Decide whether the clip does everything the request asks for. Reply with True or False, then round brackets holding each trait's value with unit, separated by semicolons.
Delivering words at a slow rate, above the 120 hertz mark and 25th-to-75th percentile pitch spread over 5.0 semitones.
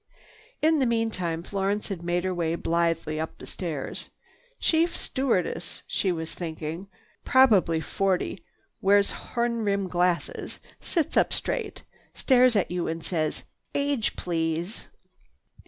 True (125 wpm; 185 Hz; 5.4 semitones)